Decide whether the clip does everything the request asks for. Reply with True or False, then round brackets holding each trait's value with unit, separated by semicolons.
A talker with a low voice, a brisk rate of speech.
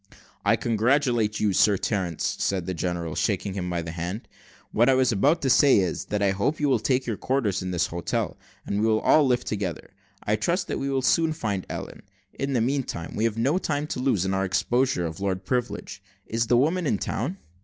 True (110 Hz; 220 wpm)